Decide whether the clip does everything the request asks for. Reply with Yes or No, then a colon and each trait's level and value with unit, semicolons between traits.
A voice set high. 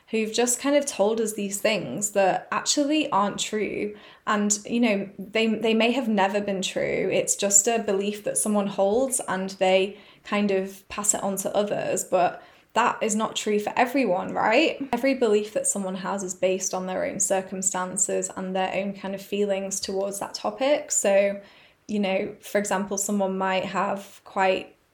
Yes: high, 200 Hz